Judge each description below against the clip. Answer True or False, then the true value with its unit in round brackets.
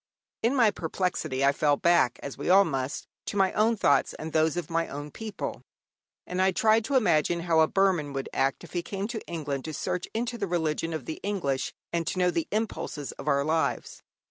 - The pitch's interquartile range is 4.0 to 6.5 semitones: True (5.1 semitones)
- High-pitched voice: False (165 Hz)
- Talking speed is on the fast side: True (215 wpm)